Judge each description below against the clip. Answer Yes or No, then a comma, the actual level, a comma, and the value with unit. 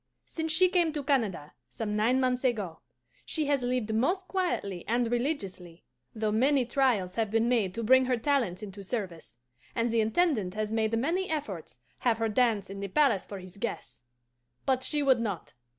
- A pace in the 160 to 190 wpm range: Yes, average, 180 wpm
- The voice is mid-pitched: No, high, 230 Hz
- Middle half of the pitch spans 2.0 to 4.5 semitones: No, average, 5.0 semitones